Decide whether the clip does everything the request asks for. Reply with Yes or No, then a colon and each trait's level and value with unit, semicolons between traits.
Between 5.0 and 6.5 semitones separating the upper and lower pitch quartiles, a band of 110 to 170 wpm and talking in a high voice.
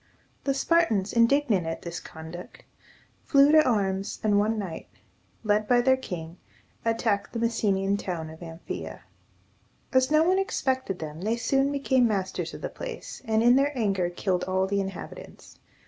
Yes: wide, 5.6 semitones; average, 165 wpm; high, 215 Hz